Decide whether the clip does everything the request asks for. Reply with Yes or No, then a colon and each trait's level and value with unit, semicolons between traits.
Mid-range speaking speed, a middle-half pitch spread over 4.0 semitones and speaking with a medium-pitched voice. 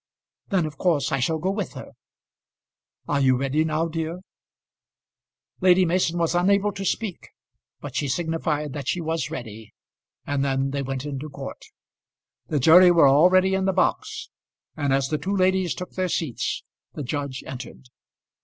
Yes: average, 165 wpm; average, 4.7 semitones; medium, 160 Hz